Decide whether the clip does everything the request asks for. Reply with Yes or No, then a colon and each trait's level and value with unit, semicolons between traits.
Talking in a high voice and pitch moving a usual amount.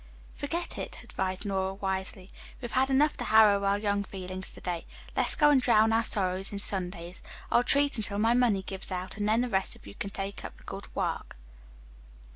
Yes: high, 200 Hz; average, 3.6 semitones